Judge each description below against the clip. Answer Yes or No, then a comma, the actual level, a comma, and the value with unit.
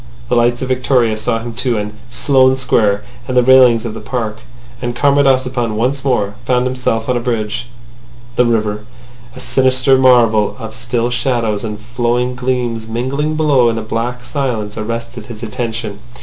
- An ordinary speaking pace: Yes, average, 170 wpm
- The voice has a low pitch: Yes, low, 120 Hz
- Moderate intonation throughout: No, narrow, 2.3 semitones